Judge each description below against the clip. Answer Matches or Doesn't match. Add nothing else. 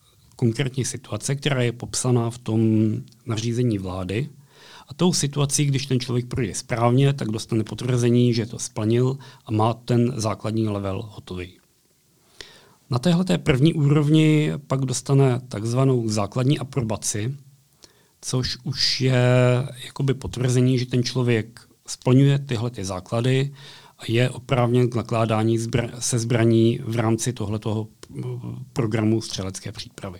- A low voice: Matches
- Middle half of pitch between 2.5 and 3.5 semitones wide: Matches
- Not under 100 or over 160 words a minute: Matches